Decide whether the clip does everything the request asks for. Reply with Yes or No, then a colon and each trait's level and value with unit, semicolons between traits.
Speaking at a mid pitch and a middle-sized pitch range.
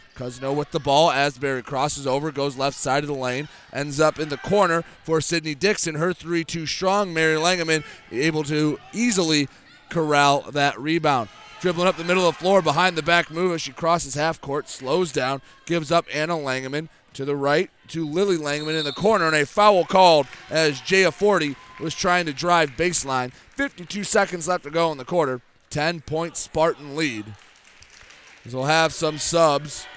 Yes: medium, 160 Hz; average, 3.3 semitones